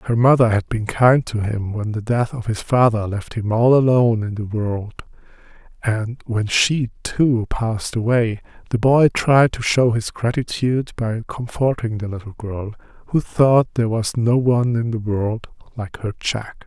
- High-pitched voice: No, low, 115 Hz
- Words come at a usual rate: Yes, average, 180 wpm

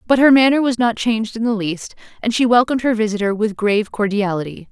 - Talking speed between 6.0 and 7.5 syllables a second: Yes, 6.3 syllables/s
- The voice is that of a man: No, female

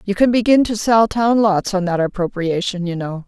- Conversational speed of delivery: No, fast, 220 wpm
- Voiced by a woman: Yes, female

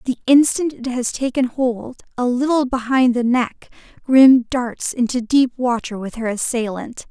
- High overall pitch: Yes, high, 245 Hz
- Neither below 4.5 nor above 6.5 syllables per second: No, 4.3 syllables/s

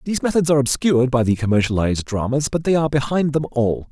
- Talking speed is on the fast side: Yes, fast, 215 wpm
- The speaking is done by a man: Yes, male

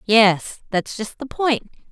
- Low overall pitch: No, high, 230 Hz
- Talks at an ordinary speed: Yes, average, 155 wpm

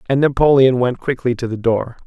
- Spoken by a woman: No, male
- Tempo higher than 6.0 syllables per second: No, 5.5 syllables/s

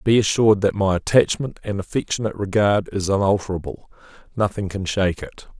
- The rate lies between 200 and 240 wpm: No, average, 150 wpm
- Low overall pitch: Yes, low, 100 Hz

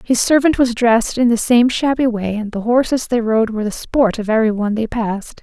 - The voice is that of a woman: Yes, female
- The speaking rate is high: Yes, fast, 230 wpm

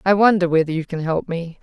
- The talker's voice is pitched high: No, medium, 175 Hz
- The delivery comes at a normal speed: No, fast, 260 wpm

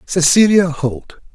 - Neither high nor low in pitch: Yes, medium, 170 Hz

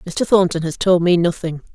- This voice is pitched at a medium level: Yes, medium, 175 Hz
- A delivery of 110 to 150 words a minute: No, fast, 205 wpm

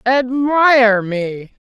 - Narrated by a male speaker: No, female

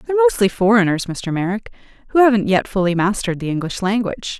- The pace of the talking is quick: No, average, 180 wpm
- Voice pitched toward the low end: No, high, 205 Hz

